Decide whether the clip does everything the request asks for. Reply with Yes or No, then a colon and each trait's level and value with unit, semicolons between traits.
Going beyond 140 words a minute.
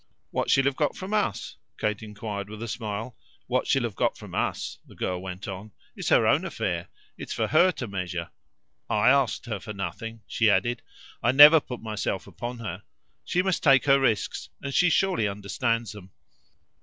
Yes: average, 195 wpm